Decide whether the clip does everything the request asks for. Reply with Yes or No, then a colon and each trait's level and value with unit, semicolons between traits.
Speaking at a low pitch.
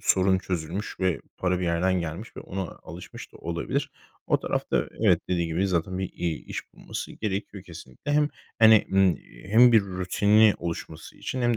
Yes: very low, 95 Hz